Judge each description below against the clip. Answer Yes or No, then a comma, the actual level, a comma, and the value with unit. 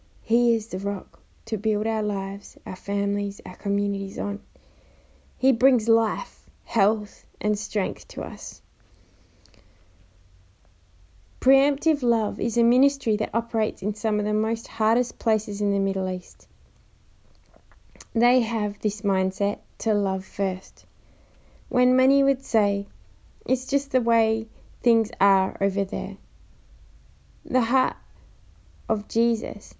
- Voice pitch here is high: Yes, high, 210 Hz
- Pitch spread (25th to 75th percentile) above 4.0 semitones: No, average, 3.4 semitones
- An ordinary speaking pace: No, slow, 125 wpm